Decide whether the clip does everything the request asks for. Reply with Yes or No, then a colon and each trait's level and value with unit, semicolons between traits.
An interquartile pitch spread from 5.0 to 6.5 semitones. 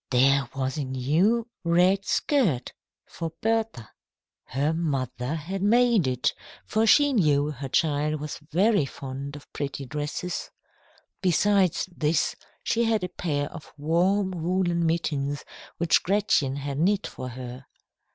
Yes: wide, 5.4 semitones